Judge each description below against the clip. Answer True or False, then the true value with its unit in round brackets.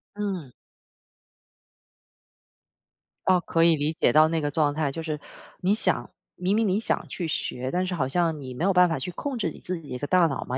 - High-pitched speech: False (165 Hz)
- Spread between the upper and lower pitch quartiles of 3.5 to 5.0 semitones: True (3.8 semitones)